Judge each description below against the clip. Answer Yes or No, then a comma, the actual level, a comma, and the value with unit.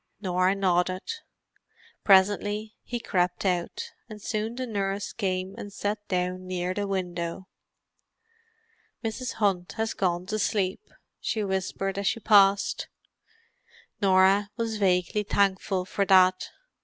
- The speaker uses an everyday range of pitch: No, narrow, 2.1 semitones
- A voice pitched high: Yes, high, 195 Hz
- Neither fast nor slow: No, slow, 120 wpm